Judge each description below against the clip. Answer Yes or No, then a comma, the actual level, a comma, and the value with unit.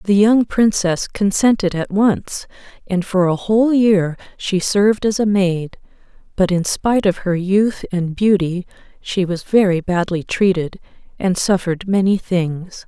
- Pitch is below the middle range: No, high, 190 Hz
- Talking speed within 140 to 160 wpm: Yes, average, 155 wpm